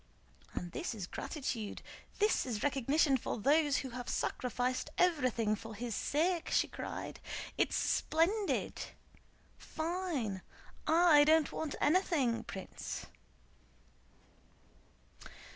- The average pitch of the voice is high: Yes, very high, 280 Hz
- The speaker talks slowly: Yes, slow, 95 wpm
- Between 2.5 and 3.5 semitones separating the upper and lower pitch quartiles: No, wide, 5.6 semitones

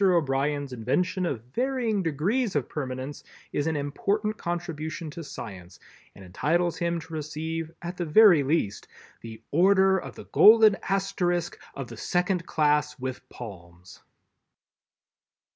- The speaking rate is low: Yes, slow, 130 wpm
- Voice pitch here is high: No, medium, 160 Hz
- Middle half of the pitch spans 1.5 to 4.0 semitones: No, average, 4.9 semitones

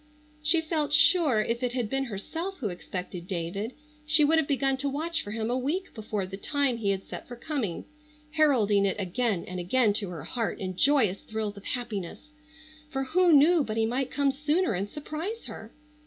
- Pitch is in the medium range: No, very high, 250 Hz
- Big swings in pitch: Yes, wide, 6.6 semitones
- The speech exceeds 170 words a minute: Yes, average, 200 wpm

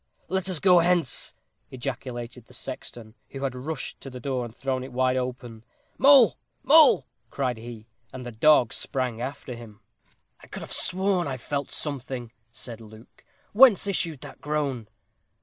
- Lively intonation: No, average, 4.0 semitones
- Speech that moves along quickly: No, average, 160 wpm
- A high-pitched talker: No, low, 130 Hz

